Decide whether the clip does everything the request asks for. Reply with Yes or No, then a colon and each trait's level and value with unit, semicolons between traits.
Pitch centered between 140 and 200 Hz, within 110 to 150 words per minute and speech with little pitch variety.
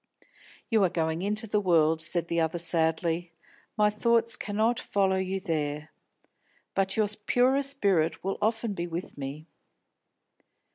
No: high, 190 Hz; average, 140 wpm; average, 4.5 semitones